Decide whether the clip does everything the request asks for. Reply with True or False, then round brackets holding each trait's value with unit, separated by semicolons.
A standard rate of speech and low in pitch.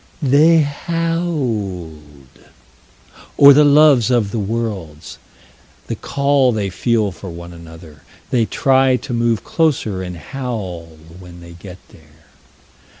False (120 wpm; 110 Hz)